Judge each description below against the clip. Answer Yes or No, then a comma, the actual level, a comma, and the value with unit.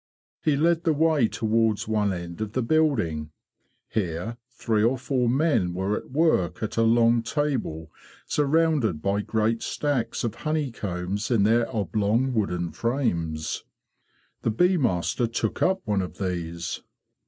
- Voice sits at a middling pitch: No, low, 115 Hz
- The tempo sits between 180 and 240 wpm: No, average, 140 wpm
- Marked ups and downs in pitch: Yes, wide, 6.0 semitones